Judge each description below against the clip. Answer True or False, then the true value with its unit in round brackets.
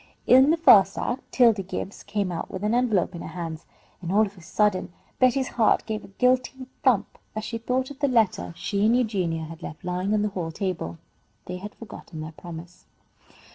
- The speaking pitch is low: False (200 Hz)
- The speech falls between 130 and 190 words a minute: False (205 wpm)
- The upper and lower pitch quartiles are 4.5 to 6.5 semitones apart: True (5.1 semitones)